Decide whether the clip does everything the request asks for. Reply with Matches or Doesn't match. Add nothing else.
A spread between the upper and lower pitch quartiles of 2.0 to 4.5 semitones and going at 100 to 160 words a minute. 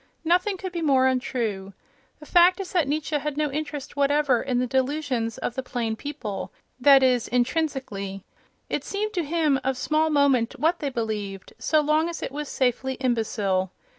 Doesn't match